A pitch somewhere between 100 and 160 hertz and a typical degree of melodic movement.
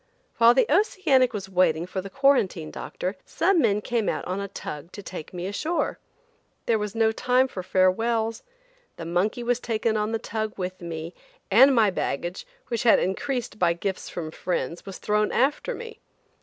No: high, 210 Hz; average, 4.7 semitones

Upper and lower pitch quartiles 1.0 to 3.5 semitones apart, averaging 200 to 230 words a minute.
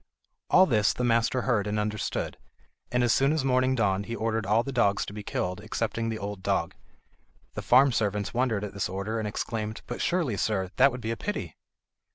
Yes: average, 3.1 semitones; fast, 205 wpm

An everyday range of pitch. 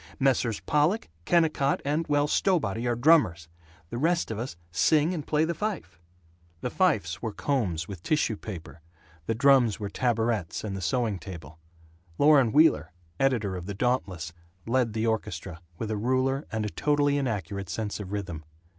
No: wide, 6.6 semitones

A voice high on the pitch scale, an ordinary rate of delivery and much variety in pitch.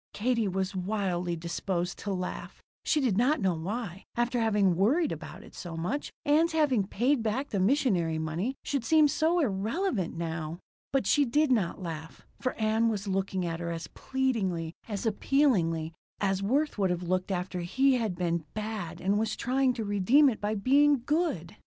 Yes: high, 205 Hz; average, 175 wpm; wide, 6.5 semitones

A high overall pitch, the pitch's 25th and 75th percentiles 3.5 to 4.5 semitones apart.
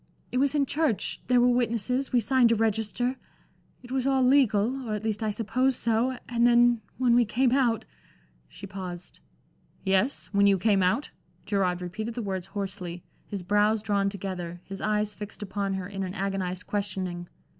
Yes: high, 210 Hz; average, 4.0 semitones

